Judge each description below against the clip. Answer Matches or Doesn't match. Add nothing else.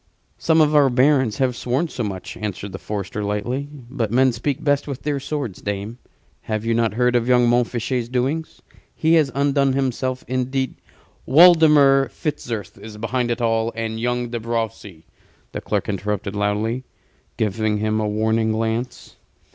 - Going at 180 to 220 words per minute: Doesn't match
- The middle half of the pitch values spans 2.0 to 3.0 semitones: Doesn't match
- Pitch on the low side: Matches